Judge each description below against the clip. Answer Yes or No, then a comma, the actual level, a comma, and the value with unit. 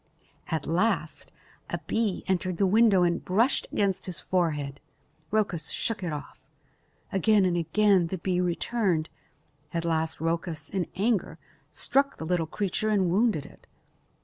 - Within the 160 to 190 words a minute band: No, average, 145 wpm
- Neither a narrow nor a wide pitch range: Yes, average, 3.8 semitones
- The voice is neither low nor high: Yes, medium, 180 Hz